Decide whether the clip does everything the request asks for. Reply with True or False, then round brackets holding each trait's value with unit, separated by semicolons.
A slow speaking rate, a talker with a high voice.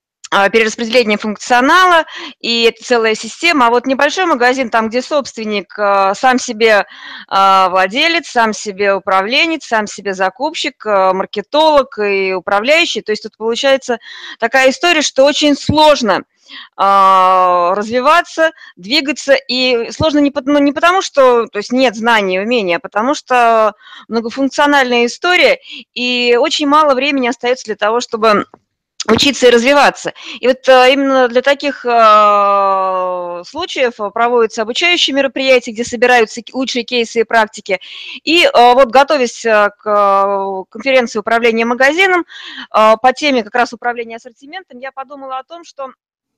False (125 wpm; 245 Hz)